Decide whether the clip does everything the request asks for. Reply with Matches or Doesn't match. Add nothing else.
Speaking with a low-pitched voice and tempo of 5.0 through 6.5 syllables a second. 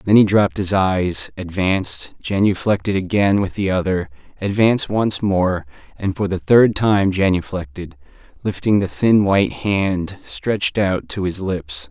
Doesn't match